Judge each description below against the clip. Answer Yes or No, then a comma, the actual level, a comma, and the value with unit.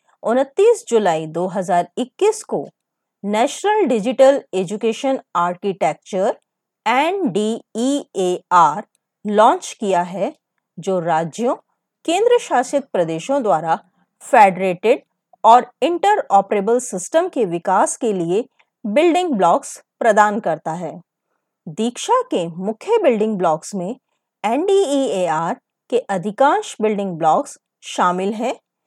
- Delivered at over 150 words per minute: No, slow, 110 wpm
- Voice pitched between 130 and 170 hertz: No, high, 225 Hz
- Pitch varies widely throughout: Yes, wide, 6.6 semitones